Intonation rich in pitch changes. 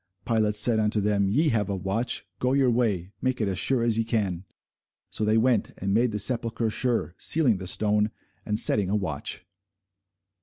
No: average, 3.0 semitones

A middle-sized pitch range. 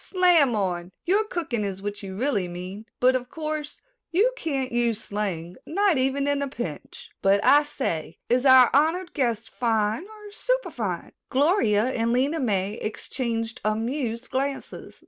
No: wide, 6.0 semitones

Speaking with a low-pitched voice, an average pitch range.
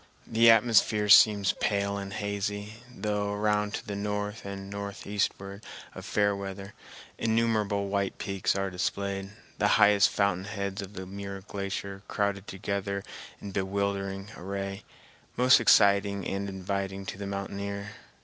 No: low, 100 Hz; narrow, 0.8 semitones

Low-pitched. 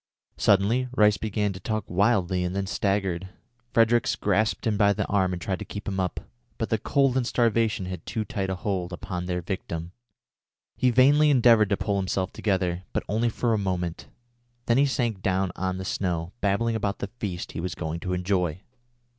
Yes: low, 100 Hz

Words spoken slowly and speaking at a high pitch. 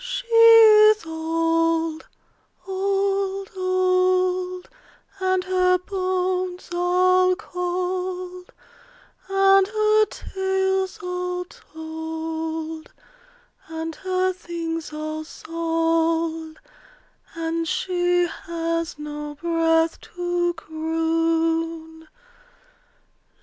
Yes: slow, 70 wpm; very high, 355 Hz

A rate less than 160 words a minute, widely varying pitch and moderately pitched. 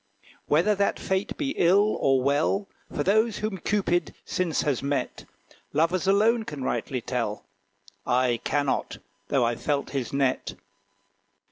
Yes: slow, 135 wpm; wide, 6.8 semitones; medium, 155 Hz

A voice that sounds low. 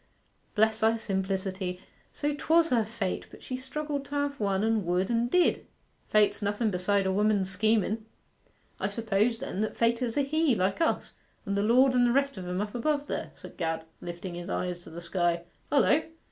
No: high, 215 Hz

